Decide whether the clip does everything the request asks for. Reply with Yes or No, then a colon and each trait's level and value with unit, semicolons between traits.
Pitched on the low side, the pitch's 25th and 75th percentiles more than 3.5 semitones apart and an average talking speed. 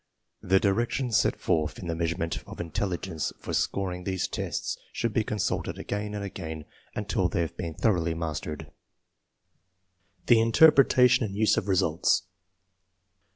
Yes: very low, 95 Hz; average, 4.3 semitones; average, 145 wpm